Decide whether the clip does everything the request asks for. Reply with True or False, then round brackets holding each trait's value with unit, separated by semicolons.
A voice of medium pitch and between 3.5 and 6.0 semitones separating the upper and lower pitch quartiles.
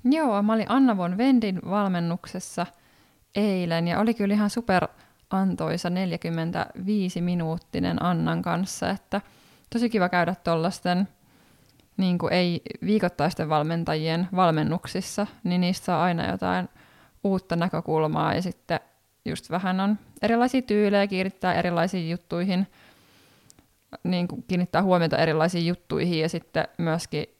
False (180 Hz; 3.0 semitones)